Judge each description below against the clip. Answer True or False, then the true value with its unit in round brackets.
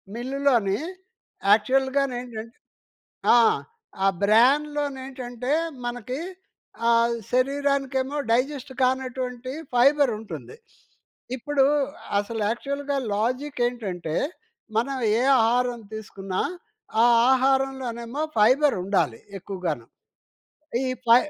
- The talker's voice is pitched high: True (250 Hz)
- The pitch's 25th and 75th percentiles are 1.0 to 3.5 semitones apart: True (2.9 semitones)